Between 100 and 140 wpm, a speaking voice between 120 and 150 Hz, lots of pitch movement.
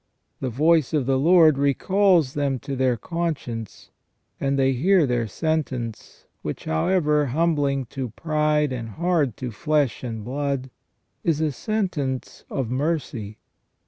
No: slow, 135 wpm; medium, 140 Hz; average, 3.8 semitones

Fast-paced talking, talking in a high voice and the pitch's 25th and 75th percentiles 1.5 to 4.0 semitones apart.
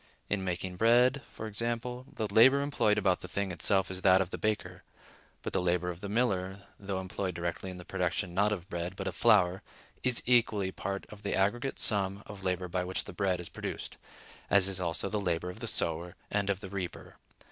No: fast, 210 wpm; very low, 95 Hz; narrow, 2.6 semitones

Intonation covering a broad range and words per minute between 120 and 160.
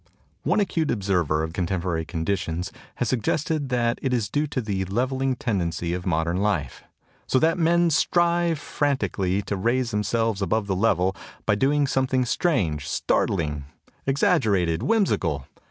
Yes: wide, 7.1 semitones; average, 150 wpm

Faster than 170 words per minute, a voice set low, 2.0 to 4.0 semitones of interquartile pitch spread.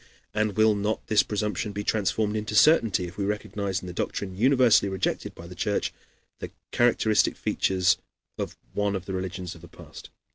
Yes: average, 180 wpm; low, 100 Hz; narrow, 2.4 semitones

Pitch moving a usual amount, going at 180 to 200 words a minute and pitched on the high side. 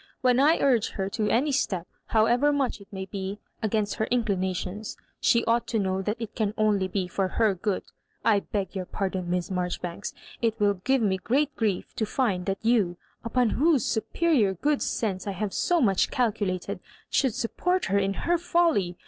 Yes: average, 4.1 semitones; average, 190 wpm; high, 210 Hz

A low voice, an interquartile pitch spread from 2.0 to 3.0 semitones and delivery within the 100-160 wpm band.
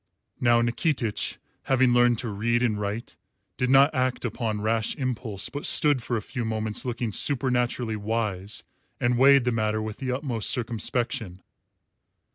Yes: low, 120 Hz; average, 2.7 semitones; average, 150 wpm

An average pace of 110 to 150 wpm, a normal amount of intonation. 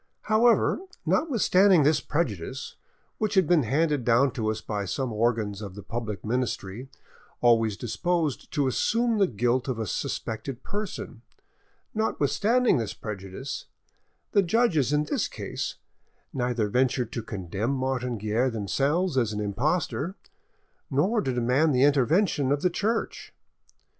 No: slow, 135 wpm; wide, 7.5 semitones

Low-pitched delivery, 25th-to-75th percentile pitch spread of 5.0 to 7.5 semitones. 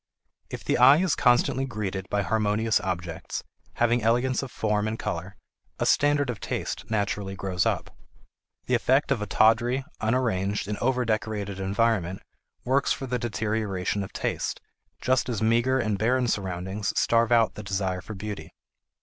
No: low, 110 Hz; average, 3.6 semitones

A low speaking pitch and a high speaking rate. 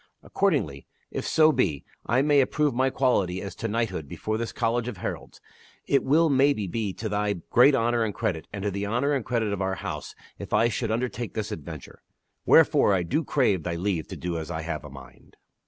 Yes: low, 110 Hz; fast, 210 wpm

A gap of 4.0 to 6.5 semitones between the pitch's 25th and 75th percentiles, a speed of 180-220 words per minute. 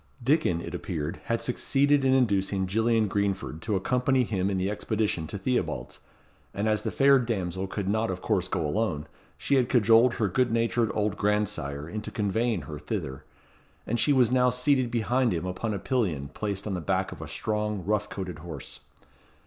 Yes: average, 4.4 semitones; average, 185 wpm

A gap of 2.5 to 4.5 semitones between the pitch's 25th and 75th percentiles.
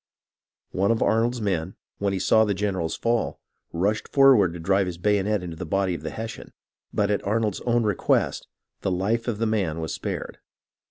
Yes: average, 3.3 semitones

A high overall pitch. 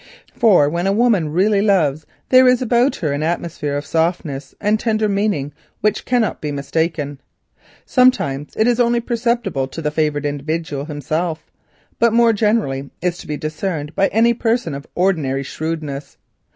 No: medium, 170 Hz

